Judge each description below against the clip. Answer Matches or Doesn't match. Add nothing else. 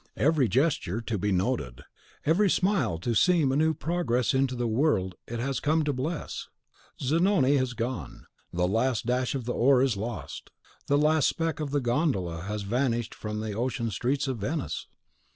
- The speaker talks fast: Doesn't match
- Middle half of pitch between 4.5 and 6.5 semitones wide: Matches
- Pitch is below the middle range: Matches